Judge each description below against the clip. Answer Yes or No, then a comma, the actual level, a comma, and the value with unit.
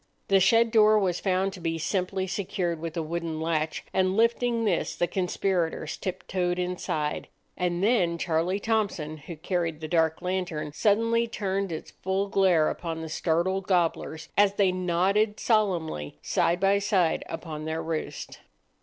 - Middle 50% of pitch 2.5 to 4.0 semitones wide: Yes, average, 3.2 semitones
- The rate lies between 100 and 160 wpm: Yes, average, 155 wpm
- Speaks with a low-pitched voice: No, medium, 180 Hz